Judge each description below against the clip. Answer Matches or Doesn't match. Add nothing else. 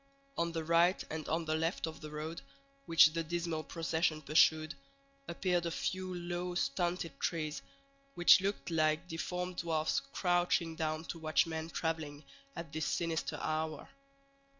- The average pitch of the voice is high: Doesn't match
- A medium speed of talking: Matches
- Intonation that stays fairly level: Matches